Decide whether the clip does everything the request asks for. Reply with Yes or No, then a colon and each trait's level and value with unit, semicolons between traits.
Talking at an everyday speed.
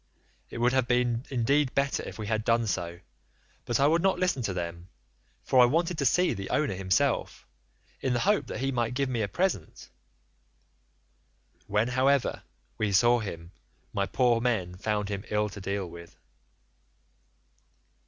Yes: average, 165 wpm